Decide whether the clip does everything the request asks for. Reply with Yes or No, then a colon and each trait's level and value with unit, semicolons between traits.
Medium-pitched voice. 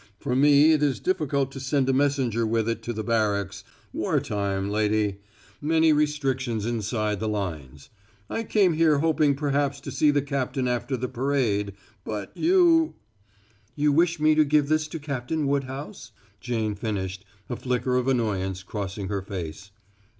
No: low, 125 Hz